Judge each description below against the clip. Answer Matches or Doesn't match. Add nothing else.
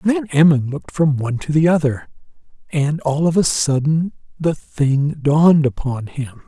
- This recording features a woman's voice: Doesn't match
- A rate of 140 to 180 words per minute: Matches